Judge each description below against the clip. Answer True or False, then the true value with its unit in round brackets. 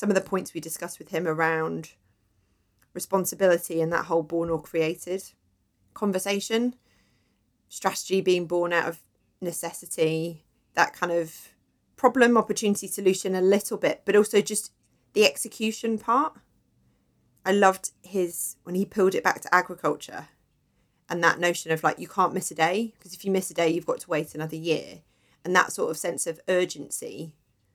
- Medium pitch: True (175 Hz)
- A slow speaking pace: False (165 wpm)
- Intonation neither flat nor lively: True (3.3 semitones)